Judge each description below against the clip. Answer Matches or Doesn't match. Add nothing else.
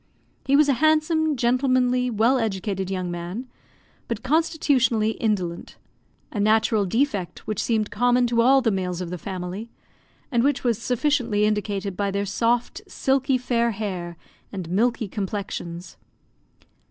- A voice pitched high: Matches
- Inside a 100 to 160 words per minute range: Matches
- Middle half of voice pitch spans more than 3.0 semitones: Matches